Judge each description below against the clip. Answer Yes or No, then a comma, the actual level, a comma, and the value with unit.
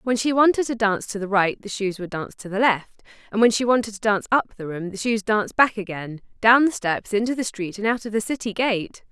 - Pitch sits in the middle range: No, high, 215 Hz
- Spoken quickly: Yes, fast, 270 wpm